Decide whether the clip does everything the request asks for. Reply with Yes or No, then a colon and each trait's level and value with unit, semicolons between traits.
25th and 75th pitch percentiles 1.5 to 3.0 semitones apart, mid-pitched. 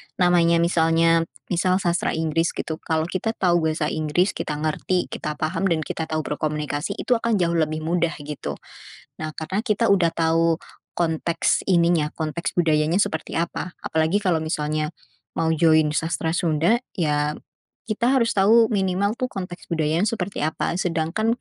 Yes: average, 2.7 semitones; medium, 165 Hz